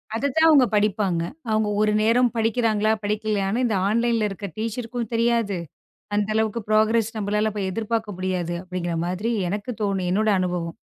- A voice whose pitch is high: Yes, high, 215 Hz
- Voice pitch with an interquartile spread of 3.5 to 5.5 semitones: No, narrow, 2.4 semitones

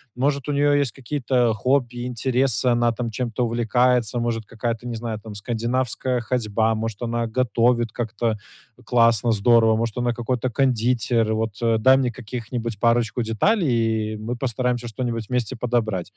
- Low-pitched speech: Yes, low, 120 Hz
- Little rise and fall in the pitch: Yes, narrow, 1.9 semitones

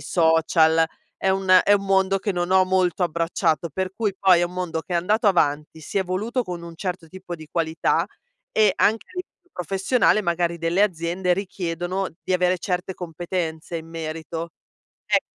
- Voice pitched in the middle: Yes, medium, 180 Hz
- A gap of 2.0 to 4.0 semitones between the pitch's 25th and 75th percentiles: Yes, narrow, 2.5 semitones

